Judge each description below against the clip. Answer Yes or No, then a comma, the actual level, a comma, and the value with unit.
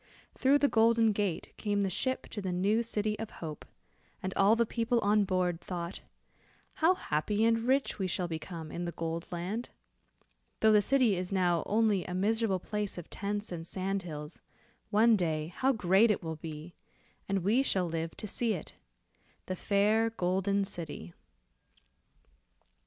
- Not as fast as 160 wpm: No, average, 165 wpm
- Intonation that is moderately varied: Yes, average, 4.1 semitones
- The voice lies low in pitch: No, high, 195 Hz